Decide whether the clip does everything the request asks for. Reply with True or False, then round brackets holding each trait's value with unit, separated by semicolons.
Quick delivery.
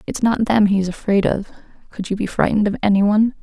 True (210 wpm)